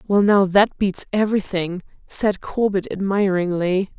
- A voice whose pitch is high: Yes, high, 195 Hz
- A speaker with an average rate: No, slow, 120 wpm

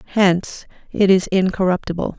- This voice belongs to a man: No, female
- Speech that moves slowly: Yes, slow, 110 wpm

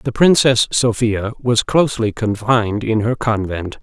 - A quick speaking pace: No, average, 140 wpm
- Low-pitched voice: Yes, low, 115 Hz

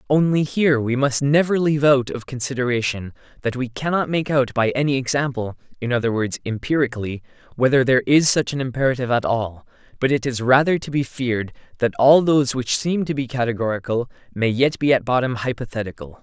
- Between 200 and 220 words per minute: No, average, 185 wpm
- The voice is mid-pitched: No, low, 130 Hz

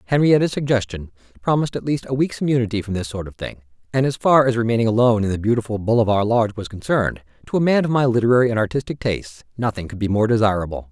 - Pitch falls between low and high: No, low, 115 Hz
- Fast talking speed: Yes, fast, 220 wpm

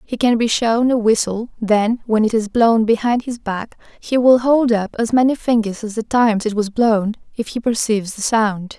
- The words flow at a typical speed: No, fast, 220 wpm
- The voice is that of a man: No, female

